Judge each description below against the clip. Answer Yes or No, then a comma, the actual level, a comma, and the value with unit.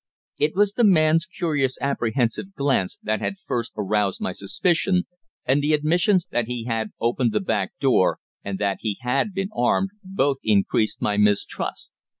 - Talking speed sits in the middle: Yes, average, 160 wpm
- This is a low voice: Yes, low, 130 Hz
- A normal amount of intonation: No, wide, 8.1 semitones